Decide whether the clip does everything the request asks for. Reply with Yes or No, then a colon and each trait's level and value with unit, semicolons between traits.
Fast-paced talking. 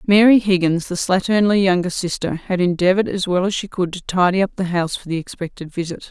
Yes: fast, 215 wpm